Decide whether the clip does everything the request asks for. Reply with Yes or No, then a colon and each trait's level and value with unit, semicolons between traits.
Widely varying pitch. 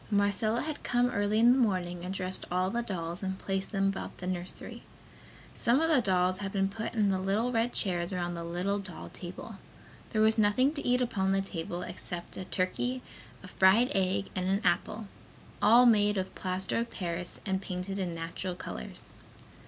No: average, 3.2 semitones